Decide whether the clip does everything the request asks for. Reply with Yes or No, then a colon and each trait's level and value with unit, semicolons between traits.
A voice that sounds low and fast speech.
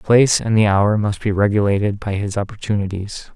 No: low, 105 Hz; average, 195 wpm